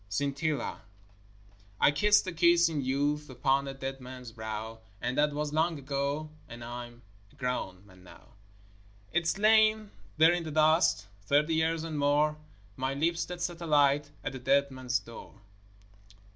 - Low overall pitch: No, medium, 145 Hz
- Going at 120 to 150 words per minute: No, average, 160 wpm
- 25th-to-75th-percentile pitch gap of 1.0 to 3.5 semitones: No, average, 3.9 semitones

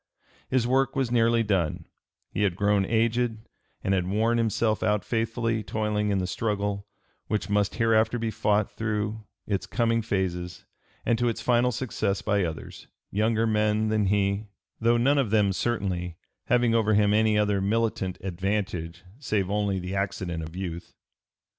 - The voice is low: Yes, low, 105 Hz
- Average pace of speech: Yes, average, 160 wpm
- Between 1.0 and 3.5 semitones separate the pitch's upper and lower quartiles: Yes, average, 2.7 semitones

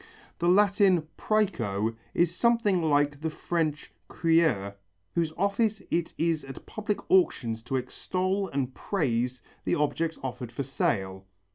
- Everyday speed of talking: No, slow, 130 wpm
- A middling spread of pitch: No, wide, 6.6 semitones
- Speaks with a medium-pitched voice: Yes, medium, 160 Hz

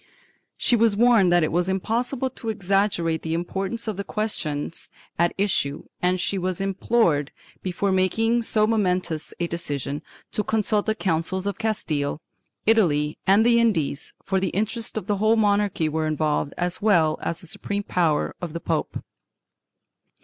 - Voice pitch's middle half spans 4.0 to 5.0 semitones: Yes, average, 4.6 semitones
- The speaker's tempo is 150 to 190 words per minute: Yes, average, 160 wpm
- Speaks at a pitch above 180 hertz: Yes, high, 190 Hz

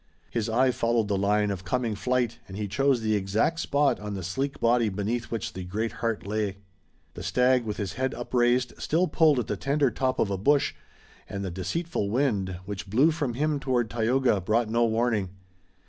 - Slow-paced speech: No, average, 195 wpm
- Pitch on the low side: Yes, low, 115 Hz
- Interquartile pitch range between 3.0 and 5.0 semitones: Yes, average, 4.0 semitones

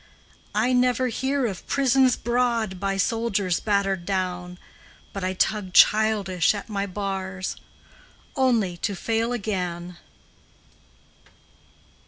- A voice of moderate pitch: No, high, 200 Hz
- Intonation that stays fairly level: No, average, 3.9 semitones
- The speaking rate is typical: No, slow, 105 wpm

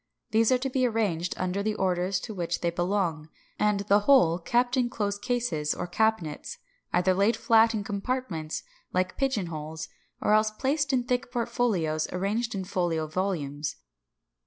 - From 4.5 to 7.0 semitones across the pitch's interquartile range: Yes, average, 5.2 semitones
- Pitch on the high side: Yes, high, 200 Hz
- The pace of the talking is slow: No, average, 160 wpm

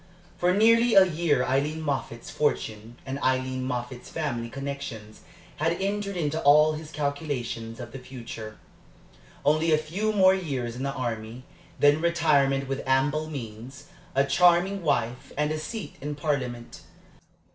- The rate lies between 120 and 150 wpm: Yes, average, 145 wpm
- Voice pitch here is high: No, medium, 140 Hz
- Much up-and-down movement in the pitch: No, average, 4.1 semitones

